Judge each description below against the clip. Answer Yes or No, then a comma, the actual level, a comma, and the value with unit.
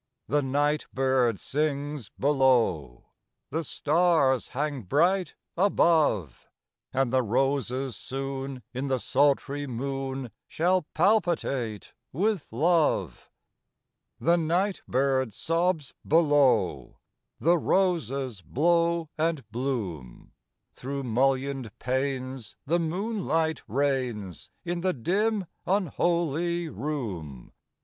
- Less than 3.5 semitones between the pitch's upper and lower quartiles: No, average, 4.7 semitones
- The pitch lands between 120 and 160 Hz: Yes, medium, 140 Hz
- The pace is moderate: No, slow, 90 wpm